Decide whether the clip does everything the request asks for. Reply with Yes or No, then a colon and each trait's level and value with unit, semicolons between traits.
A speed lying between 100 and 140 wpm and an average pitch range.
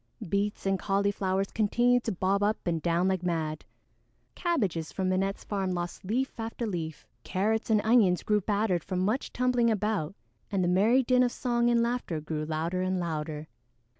No: average, 170 wpm; average, 4.2 semitones